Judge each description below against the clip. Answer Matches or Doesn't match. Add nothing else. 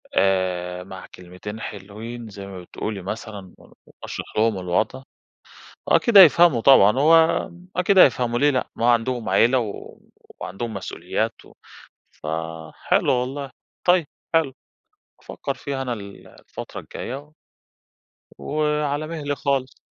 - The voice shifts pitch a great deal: Matches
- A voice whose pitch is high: Doesn't match